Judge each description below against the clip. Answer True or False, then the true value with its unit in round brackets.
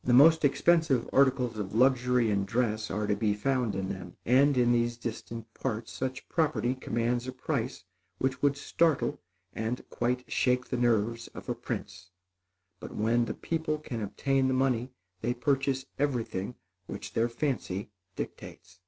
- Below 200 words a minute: True (160 wpm)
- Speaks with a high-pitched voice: False (125 Hz)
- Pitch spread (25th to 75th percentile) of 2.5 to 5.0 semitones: True (3.1 semitones)